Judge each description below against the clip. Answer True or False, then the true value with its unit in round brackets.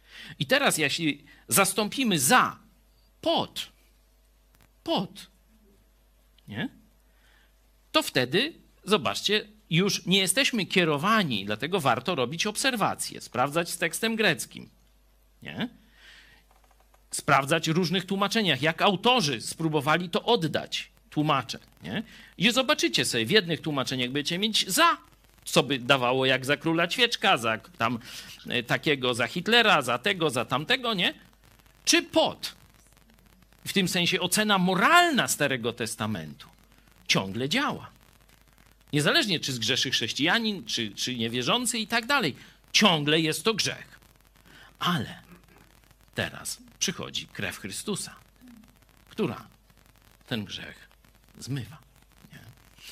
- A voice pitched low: False (175 Hz)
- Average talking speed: False (105 wpm)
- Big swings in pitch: True (7.8 semitones)